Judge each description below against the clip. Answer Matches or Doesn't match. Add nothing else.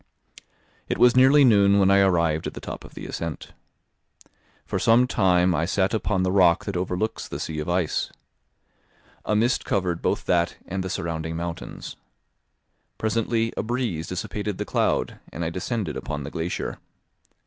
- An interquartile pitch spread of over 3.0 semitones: Matches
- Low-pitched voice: Matches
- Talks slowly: Doesn't match